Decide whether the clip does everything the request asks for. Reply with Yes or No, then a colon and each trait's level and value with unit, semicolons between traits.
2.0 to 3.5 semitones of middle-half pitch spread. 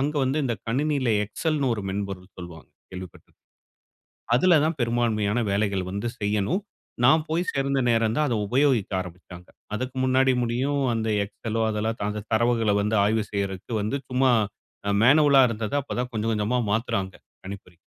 No: average, 4.4 semitones